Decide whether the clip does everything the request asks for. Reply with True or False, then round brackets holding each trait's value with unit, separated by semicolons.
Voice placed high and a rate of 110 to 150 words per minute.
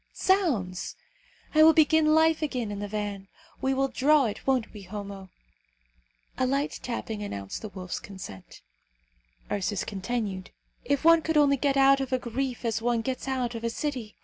False (245 Hz; 175 wpm)